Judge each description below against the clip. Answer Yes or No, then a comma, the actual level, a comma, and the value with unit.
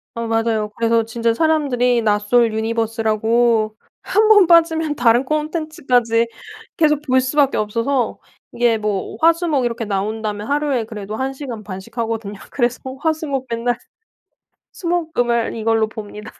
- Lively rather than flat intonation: No, average, 4.4 semitones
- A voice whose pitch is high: Yes, high, 235 Hz